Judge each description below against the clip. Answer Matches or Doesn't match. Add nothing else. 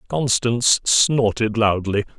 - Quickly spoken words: Doesn't match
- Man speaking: Matches